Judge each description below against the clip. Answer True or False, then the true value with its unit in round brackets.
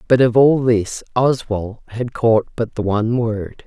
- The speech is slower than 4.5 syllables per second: True (4.0 syllables/s)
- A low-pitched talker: True (115 Hz)